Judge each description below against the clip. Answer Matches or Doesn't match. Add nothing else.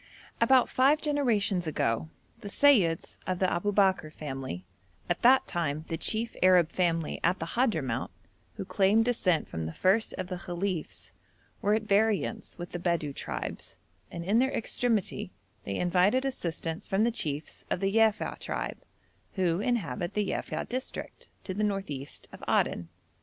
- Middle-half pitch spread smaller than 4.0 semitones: Doesn't match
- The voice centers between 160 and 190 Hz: Matches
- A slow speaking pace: Doesn't match